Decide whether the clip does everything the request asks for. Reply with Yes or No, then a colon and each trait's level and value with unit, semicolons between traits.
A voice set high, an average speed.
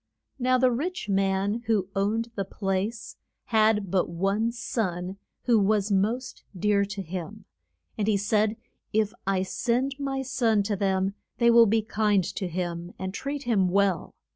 Yes: high, 210 Hz; average, 160 wpm